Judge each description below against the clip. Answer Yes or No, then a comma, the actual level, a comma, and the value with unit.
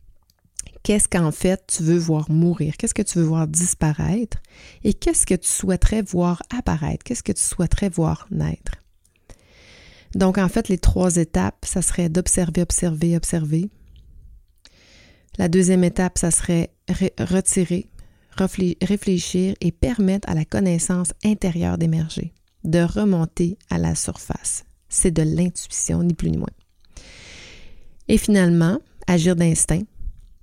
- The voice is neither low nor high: Yes, medium, 175 Hz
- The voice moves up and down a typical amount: Yes, average, 3.1 semitones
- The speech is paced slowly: Yes, slow, 135 wpm